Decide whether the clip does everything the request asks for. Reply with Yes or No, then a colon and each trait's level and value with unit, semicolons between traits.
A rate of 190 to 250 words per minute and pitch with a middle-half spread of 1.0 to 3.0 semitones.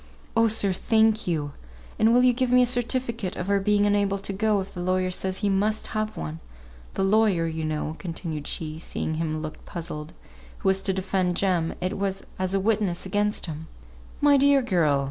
No: fast, 205 wpm; average, 4.4 semitones